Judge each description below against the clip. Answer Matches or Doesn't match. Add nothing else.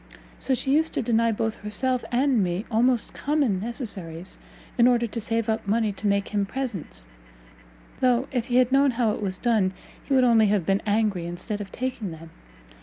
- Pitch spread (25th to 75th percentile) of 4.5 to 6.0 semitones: Doesn't match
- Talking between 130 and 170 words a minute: Doesn't match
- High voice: Matches